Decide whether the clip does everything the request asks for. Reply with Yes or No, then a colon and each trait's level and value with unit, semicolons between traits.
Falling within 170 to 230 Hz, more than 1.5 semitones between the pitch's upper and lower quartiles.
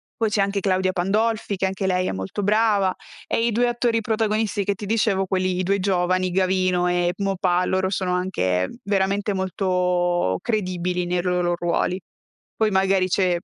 Yes: high, 190 Hz; narrow, 2.1 semitones